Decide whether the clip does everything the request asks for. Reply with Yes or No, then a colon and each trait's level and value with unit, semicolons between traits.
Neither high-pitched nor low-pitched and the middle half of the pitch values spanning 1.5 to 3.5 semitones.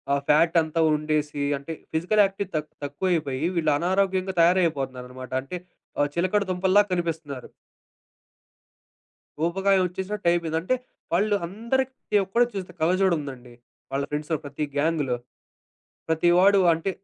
No: medium, 170 Hz; average, 4.2 semitones